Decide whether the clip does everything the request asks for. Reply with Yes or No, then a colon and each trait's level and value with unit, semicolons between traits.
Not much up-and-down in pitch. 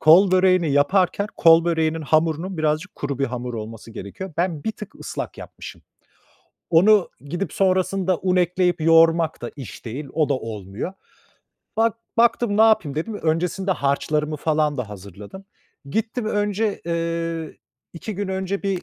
No: average, 4.4 semitones